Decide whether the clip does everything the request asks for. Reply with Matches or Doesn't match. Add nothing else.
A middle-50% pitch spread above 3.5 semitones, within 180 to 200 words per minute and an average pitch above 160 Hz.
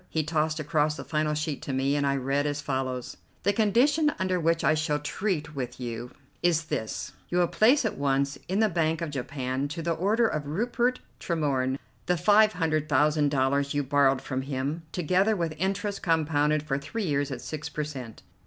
Doesn't match